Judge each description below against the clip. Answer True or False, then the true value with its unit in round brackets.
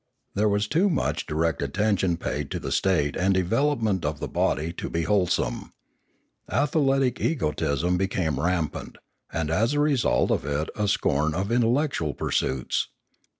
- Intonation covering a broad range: True (6.9 semitones)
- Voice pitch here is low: True (95 Hz)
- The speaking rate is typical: True (150 wpm)